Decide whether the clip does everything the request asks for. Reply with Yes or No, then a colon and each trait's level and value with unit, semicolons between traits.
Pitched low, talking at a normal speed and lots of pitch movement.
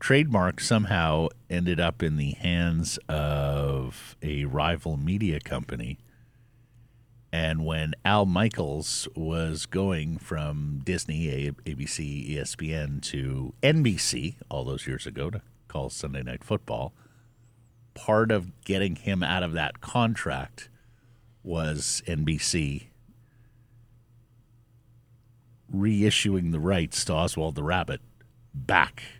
No: very low, 95 Hz; slow, 105 wpm; wide, 7.0 semitones